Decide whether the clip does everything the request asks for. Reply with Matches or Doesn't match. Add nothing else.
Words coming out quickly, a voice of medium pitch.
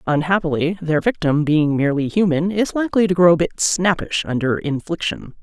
Doesn't match